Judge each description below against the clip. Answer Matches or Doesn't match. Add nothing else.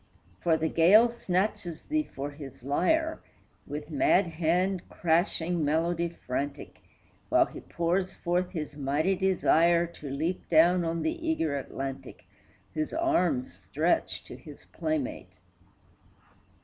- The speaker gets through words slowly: Matches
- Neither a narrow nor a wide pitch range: Matches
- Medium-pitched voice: Matches